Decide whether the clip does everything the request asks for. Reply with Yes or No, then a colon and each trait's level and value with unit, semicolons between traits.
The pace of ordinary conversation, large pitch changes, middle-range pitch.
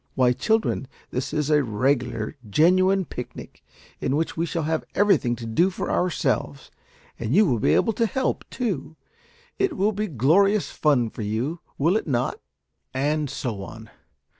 Yes: average, 165 wpm; wide, 7.2 semitones; medium, 150 Hz